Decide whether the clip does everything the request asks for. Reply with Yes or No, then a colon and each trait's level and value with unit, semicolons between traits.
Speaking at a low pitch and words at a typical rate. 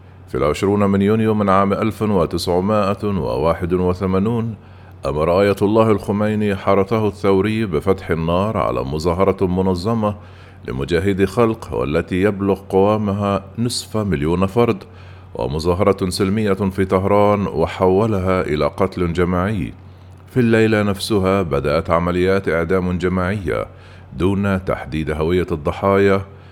Yes: very low, 95 Hz; average, 100 wpm